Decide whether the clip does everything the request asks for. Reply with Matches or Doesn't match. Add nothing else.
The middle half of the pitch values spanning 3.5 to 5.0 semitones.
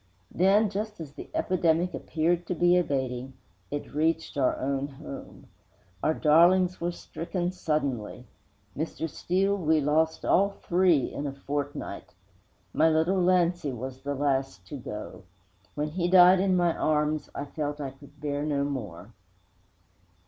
Matches